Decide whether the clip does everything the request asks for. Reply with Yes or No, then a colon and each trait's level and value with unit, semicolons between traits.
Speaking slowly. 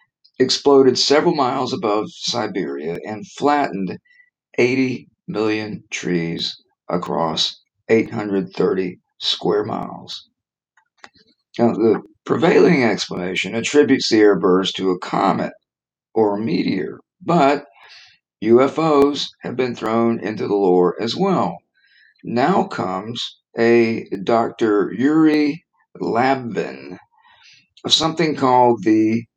Yes: slow, 100 wpm